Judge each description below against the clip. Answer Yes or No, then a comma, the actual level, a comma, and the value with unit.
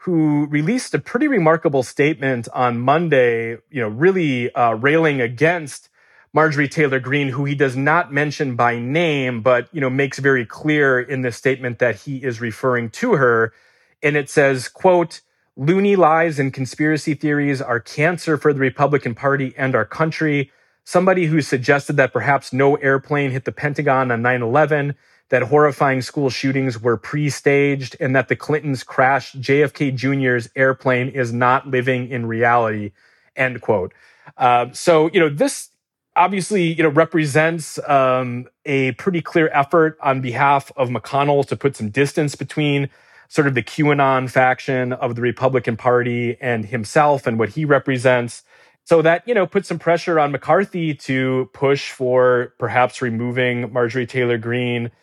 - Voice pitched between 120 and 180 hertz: Yes, low, 135 Hz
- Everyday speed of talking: Yes, average, 160 wpm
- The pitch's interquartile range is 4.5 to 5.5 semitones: No, average, 3.3 semitones